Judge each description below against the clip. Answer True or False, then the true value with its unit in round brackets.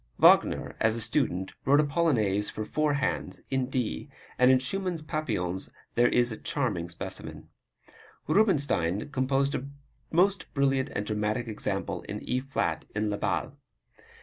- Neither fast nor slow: True (150 wpm)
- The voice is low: True (130 Hz)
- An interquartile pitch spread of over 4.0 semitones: True (5.2 semitones)